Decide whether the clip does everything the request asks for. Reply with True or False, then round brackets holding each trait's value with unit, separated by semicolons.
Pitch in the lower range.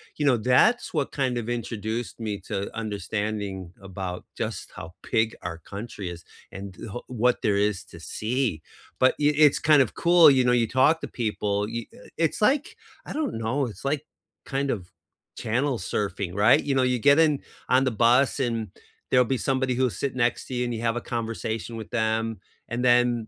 True (120 Hz)